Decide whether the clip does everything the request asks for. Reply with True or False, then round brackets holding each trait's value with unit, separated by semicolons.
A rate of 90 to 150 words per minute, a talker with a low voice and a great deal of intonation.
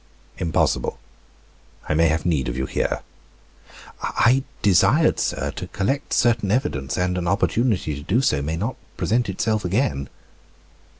True (140 wpm; 90 Hz; 6.7 semitones)